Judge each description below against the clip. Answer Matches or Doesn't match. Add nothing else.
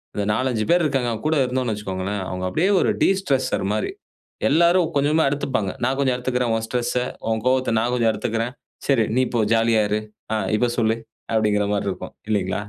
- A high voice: Doesn't match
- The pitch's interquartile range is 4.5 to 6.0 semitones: Doesn't match